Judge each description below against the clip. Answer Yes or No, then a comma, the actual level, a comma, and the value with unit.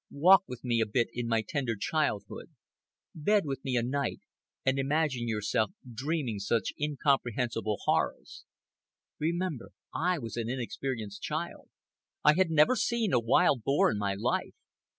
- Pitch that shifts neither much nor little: Yes, average, 5.0 semitones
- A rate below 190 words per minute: Yes, average, 150 wpm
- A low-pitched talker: Yes, low, 130 Hz